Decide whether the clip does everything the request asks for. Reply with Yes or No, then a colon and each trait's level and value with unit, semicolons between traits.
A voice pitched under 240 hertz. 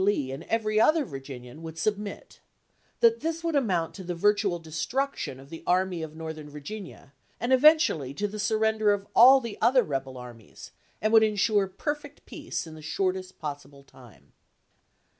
Yes: high, 190 Hz